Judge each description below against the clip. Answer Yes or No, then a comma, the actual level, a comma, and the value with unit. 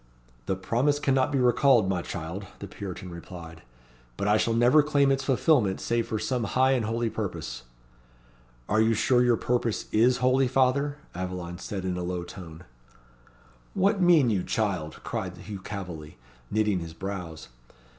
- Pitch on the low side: Yes, low, 110 Hz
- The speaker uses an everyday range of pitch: No, wide, 5.9 semitones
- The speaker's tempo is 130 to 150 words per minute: No, average, 160 wpm